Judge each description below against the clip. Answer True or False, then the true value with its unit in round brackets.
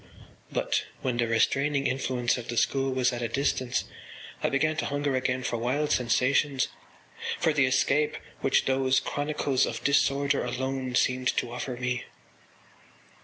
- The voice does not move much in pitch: True (2.1 semitones)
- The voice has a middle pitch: False (130 Hz)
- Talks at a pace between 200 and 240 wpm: False (150 wpm)